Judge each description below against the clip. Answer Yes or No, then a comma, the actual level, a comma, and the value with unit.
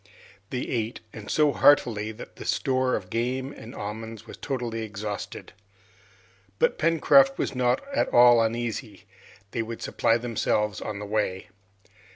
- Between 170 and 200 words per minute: No, average, 145 wpm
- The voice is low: Yes, low, 115 Hz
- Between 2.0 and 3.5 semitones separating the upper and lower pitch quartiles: Yes, average, 3.0 semitones